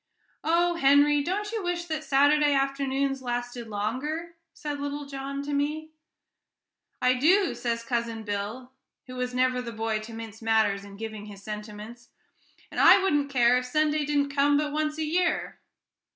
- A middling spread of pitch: Yes, average, 4.4 semitones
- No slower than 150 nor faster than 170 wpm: Yes, average, 165 wpm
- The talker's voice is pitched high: Yes, very high, 275 Hz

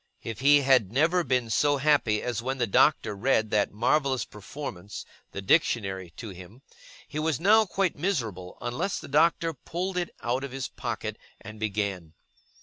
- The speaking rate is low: No, average, 165 wpm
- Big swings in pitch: Yes, wide, 6.2 semitones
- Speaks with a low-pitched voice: Yes, low, 125 Hz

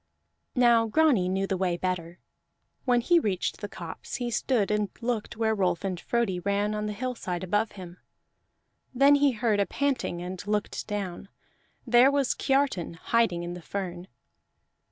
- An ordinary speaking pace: Yes, average, 160 wpm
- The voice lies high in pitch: Yes, high, 210 Hz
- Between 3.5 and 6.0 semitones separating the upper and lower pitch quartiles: Yes, average, 4.7 semitones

